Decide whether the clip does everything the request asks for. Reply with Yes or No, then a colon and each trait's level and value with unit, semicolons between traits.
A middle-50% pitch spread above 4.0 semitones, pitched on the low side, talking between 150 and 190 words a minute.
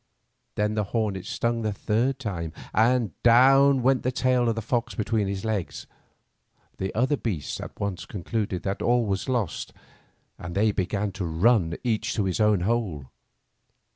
No: average, 3.7 semitones; low, 110 Hz; average, 165 wpm